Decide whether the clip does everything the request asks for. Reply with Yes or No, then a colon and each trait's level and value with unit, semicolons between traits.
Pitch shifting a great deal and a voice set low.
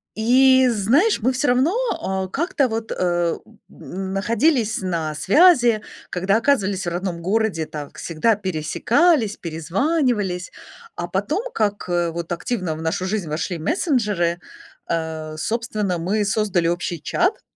No: wide, 5.7 semitones; high, 195 Hz